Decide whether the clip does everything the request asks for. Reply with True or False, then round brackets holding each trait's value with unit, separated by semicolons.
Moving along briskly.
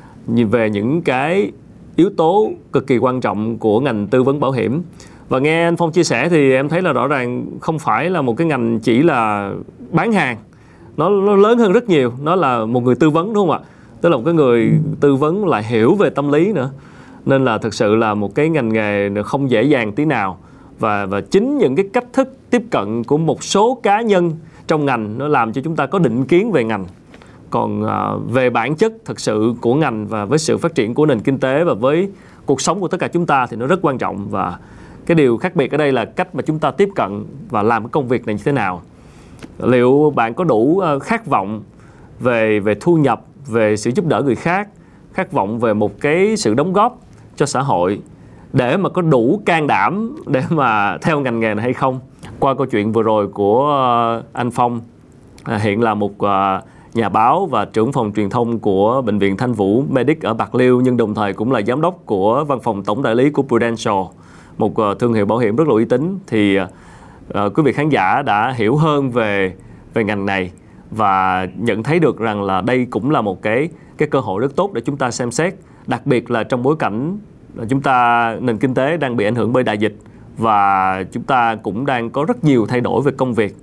False (225 wpm)